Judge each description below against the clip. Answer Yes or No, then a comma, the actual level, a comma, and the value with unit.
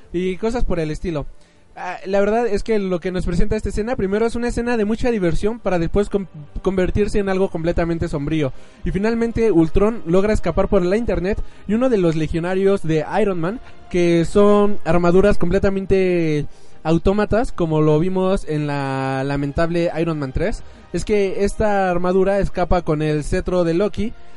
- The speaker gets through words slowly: No, average, 170 wpm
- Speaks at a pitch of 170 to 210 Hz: Yes, medium, 185 Hz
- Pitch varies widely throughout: No, average, 3.5 semitones